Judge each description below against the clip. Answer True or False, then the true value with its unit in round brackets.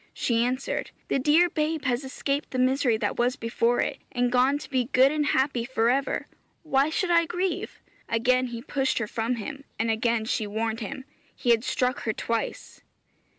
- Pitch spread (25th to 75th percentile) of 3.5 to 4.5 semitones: False (3.1 semitones)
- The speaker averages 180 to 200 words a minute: True (190 wpm)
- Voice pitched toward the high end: True (255 Hz)